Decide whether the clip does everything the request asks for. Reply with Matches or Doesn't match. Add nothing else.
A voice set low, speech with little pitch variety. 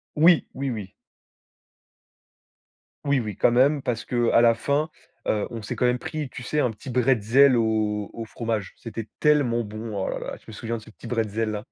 Doesn't match